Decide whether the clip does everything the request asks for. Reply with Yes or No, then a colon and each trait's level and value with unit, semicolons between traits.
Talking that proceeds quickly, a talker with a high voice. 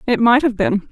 Yes: fast, 260 wpm; high, 235 Hz